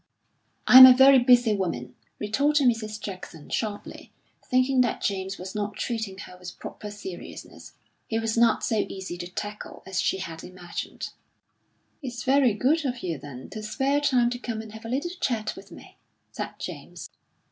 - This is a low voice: No, high, 220 Hz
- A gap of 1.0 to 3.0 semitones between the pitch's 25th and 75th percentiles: No, average, 4.8 semitones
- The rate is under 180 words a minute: Yes, average, 170 wpm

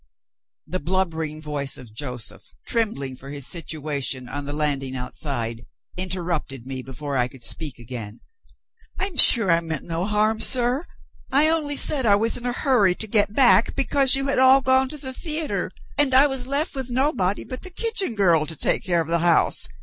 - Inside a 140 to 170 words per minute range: No, average, 190 wpm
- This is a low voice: No, medium, 185 Hz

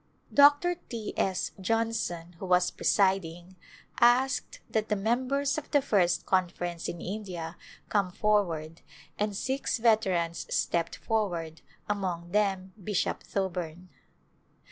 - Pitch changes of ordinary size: Yes, average, 4.2 semitones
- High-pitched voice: Yes, high, 195 Hz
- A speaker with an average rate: No, slow, 120 wpm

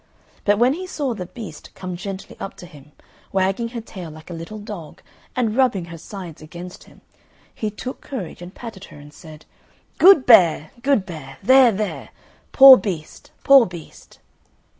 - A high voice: Yes, high, 195 Hz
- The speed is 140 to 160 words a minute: No, average, 170 wpm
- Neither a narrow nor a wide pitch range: No, wide, 5.9 semitones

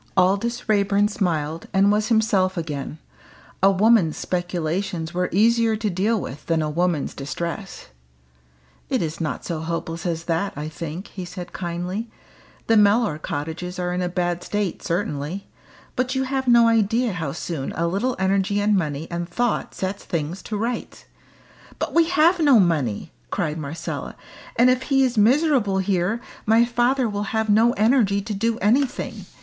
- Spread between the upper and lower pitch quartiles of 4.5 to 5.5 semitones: Yes, average, 5.0 semitones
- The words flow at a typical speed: Yes, average, 165 wpm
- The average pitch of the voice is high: Yes, high, 195 Hz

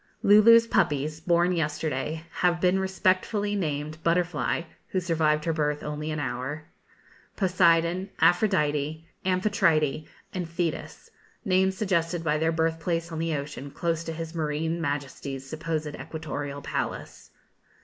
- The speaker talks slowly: Yes, slow, 130 wpm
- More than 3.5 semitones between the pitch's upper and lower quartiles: No, average, 2.9 semitones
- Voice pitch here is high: No, medium, 165 Hz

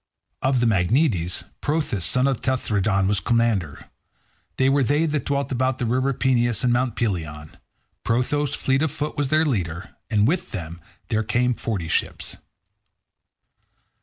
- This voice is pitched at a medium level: No, low, 120 Hz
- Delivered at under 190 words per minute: Yes, average, 150 wpm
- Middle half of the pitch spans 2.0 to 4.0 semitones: No, average, 5.3 semitones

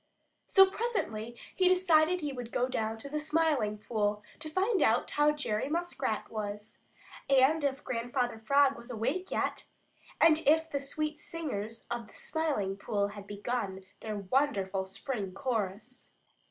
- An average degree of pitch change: No, wide, 6.4 semitones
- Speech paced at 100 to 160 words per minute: Yes, average, 155 wpm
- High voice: Yes, very high, 255 Hz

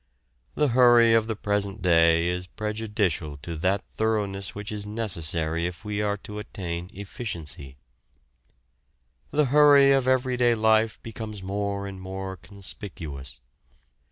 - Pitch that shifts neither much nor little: Yes, average, 3.8 semitones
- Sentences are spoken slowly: Yes, slow, 125 wpm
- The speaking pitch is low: Yes, low, 100 Hz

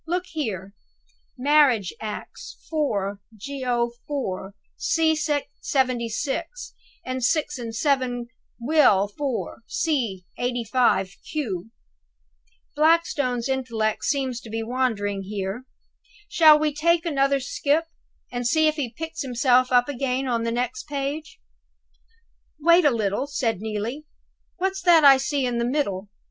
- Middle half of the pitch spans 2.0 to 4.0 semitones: No, average, 4.7 semitones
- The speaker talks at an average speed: No, slow, 125 wpm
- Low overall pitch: No, very high, 255 Hz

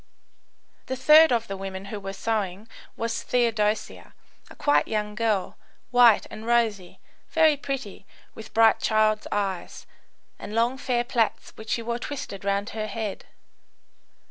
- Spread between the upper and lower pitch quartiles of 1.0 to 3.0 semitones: Yes, average, 2.7 semitones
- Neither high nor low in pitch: No, high, 220 Hz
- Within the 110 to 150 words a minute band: Yes, average, 145 wpm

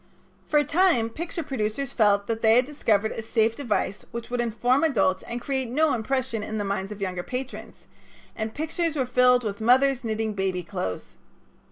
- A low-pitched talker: No, high, 235 Hz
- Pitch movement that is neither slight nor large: Yes, average, 3.9 semitones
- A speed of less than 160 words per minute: No, average, 185 wpm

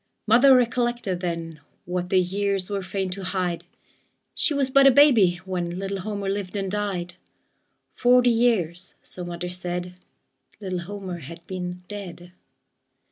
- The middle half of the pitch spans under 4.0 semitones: Yes, average, 2.7 semitones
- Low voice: No, high, 190 Hz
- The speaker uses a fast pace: No, average, 140 wpm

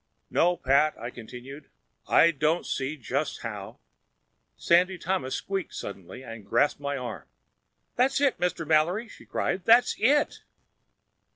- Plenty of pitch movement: Yes, wide, 5.9 semitones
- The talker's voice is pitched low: No, medium, 155 Hz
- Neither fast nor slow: No, slow, 130 wpm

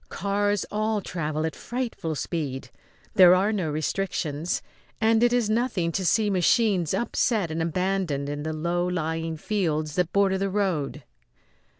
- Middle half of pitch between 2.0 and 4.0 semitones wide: No, average, 4.5 semitones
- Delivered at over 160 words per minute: No, average, 150 wpm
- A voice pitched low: No, medium, 180 Hz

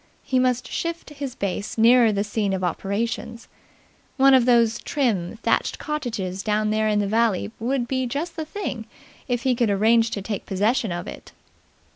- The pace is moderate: Yes, average, 175 wpm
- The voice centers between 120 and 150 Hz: No, high, 230 Hz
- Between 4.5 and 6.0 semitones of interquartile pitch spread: No, average, 3.6 semitones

